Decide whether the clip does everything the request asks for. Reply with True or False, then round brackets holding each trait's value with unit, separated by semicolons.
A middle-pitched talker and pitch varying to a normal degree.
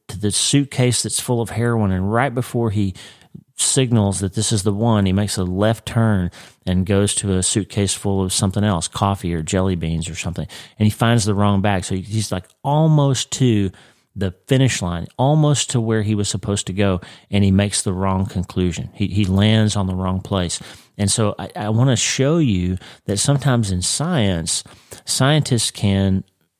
False (105 Hz; 3.6 semitones)